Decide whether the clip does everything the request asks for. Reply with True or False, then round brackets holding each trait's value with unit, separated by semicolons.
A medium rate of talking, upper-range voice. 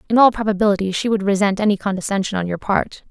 False (215 wpm; 200 Hz)